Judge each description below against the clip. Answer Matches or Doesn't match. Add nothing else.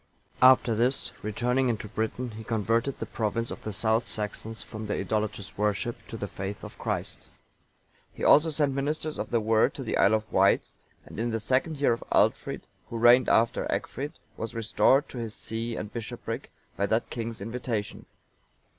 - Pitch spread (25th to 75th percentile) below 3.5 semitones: Matches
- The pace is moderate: Matches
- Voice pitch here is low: Matches